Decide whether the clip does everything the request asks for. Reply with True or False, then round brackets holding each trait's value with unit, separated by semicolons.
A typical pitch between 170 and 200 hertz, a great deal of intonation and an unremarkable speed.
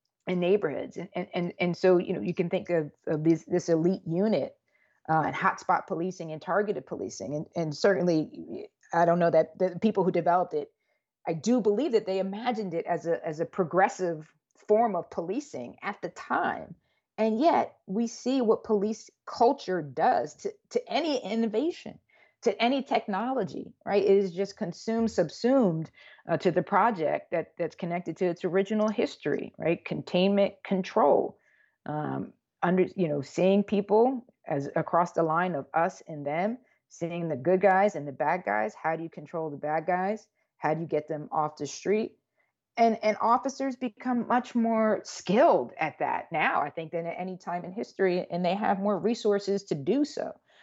False (185 Hz; 4.4 semitones; 180 wpm)